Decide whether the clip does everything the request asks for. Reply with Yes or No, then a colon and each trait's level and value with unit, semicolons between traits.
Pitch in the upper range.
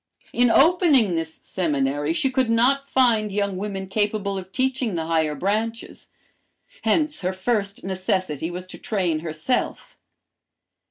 Yes: high, 200 Hz